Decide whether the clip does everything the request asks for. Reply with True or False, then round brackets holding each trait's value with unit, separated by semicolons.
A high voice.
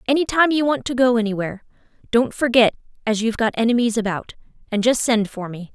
True (230 Hz)